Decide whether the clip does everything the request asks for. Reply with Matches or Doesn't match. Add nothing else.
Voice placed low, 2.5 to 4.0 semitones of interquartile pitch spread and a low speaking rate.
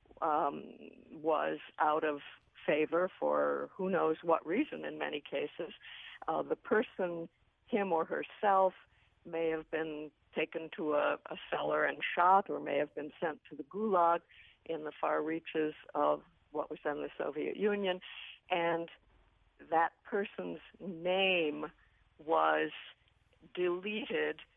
Doesn't match